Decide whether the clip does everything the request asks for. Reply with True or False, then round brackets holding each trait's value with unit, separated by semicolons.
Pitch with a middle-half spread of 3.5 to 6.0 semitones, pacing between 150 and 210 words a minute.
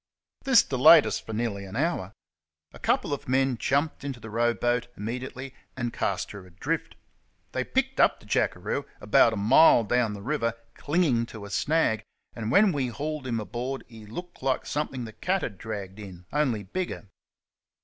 True (4.6 semitones; 175 wpm)